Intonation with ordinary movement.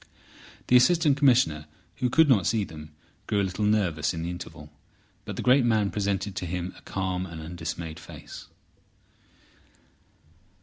No: wide, 5.7 semitones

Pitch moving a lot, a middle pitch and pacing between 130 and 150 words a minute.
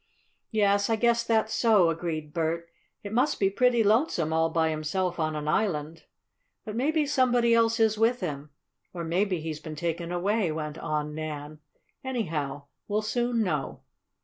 No: wide, 6.3 semitones; medium, 180 Hz; average, 160 wpm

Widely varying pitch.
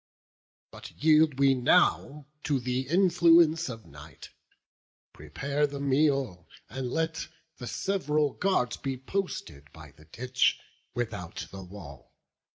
Yes: wide, 6.8 semitones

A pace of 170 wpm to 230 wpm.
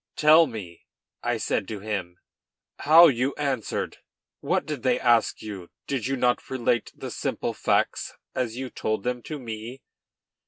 No: average, 155 wpm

